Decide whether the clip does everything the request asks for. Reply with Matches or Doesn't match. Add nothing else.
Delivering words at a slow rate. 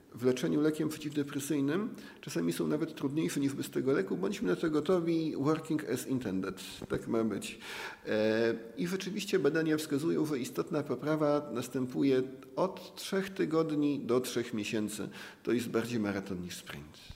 Doesn't match